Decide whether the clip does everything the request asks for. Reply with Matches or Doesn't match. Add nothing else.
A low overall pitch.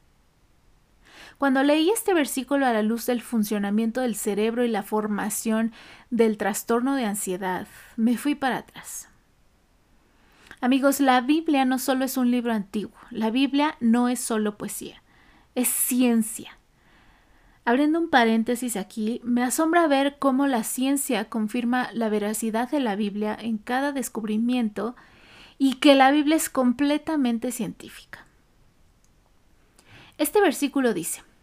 Doesn't match